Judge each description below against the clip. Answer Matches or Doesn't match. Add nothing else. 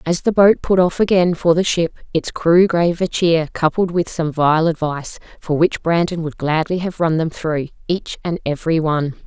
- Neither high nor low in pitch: Matches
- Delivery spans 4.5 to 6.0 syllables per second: Matches